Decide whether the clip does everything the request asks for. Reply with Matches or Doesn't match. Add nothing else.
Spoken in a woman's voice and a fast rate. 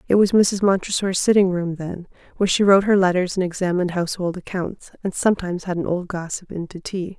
Matches